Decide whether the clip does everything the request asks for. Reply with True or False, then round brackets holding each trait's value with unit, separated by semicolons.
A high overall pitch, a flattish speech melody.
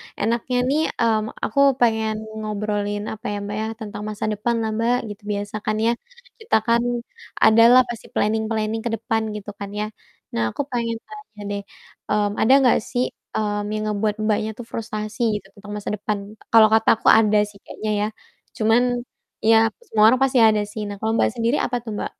True (220 Hz; 1.6 semitones)